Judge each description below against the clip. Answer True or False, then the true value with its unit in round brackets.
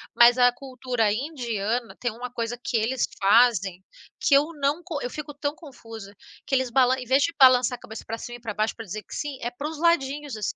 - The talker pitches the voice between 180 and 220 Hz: False (245 Hz)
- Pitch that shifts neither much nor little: True (3.5 semitones)